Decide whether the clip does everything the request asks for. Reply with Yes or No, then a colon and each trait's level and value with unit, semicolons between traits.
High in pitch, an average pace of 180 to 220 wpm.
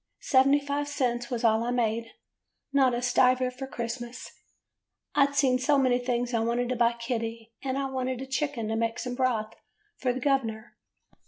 Yes: very high, 250 Hz; average, 190 wpm